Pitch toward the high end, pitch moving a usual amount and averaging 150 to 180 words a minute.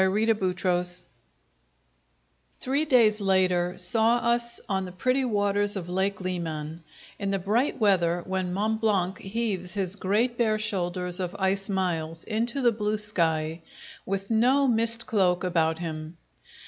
No: high, 195 Hz; average, 3.6 semitones; average, 140 wpm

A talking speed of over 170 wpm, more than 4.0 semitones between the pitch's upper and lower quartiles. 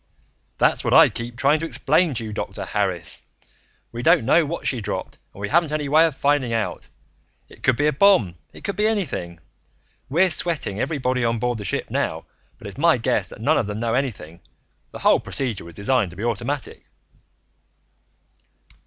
Yes: average, 190 wpm; wide, 5.4 semitones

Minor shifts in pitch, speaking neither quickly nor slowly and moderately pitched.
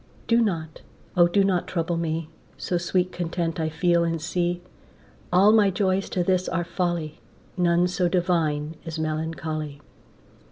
Yes: narrow, 2.0 semitones; average, 150 wpm; medium, 175 Hz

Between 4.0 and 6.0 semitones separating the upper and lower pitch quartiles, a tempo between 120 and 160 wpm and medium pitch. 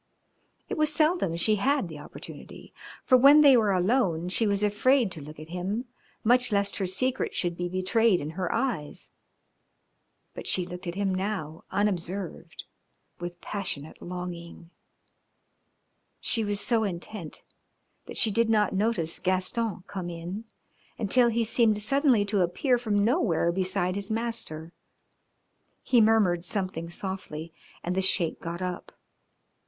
No: average, 4.4 semitones; average, 145 wpm; high, 195 Hz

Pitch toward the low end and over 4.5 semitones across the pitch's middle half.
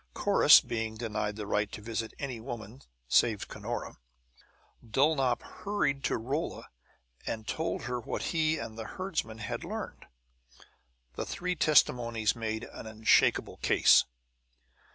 No: low, 115 Hz; average, 4.0 semitones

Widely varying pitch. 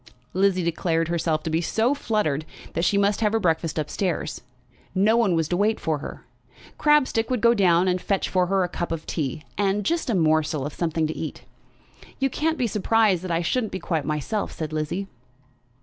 No: average, 4.8 semitones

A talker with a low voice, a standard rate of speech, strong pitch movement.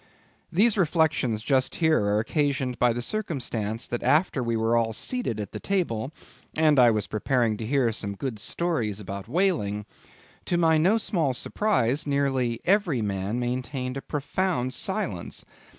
Yes: low, 130 Hz; average, 155 wpm; wide, 6.0 semitones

